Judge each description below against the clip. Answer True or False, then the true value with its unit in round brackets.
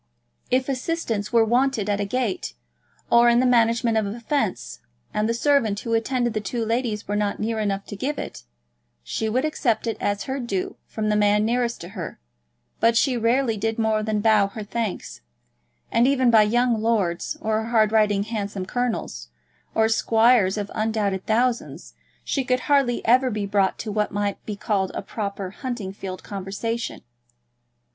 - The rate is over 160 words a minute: True (175 wpm)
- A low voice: False (220 Hz)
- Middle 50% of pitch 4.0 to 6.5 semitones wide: False (2.8 semitones)